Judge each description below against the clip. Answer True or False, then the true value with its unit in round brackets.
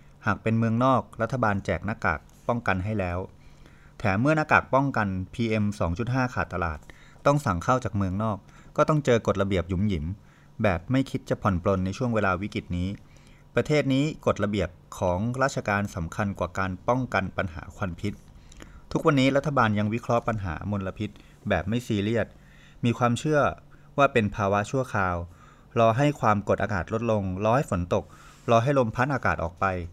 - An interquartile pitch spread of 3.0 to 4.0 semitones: False (5.0 semitones)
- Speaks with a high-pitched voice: False (105 Hz)